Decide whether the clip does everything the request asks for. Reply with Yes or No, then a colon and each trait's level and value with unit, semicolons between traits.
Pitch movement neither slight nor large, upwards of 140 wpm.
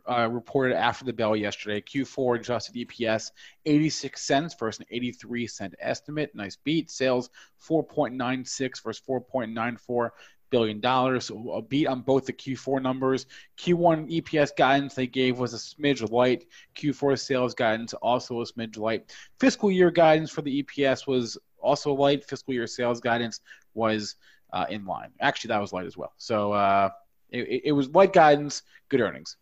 Yes: average, 3.4 semitones; average, 165 wpm